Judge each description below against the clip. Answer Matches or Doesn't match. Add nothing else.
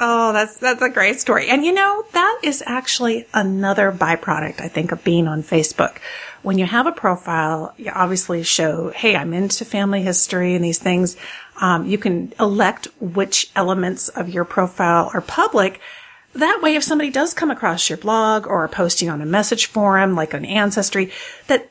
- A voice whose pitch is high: Matches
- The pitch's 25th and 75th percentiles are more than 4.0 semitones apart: Matches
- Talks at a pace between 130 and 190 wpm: Matches